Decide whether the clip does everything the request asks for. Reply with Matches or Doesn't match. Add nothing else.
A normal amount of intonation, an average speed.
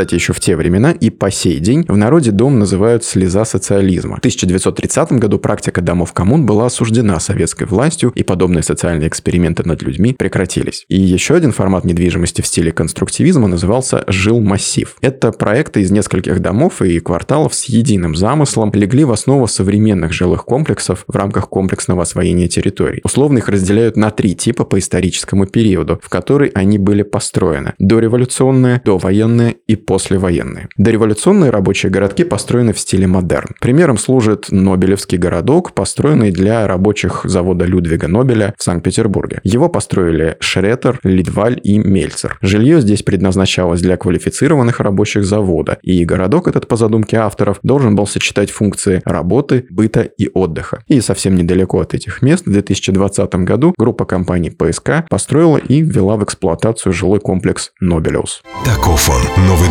Matches